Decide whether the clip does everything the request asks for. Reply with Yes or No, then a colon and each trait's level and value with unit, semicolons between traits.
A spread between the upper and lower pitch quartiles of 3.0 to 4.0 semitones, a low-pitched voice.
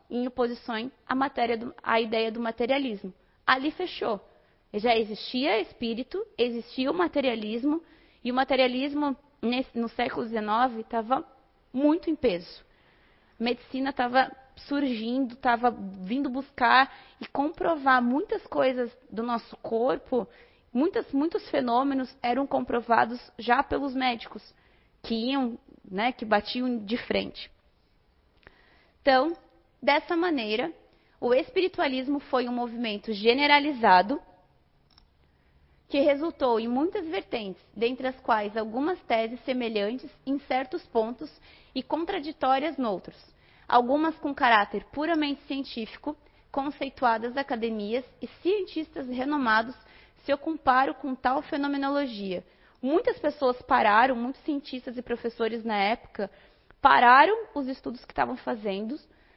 No: average, 3.4 semitones; very high, 260 Hz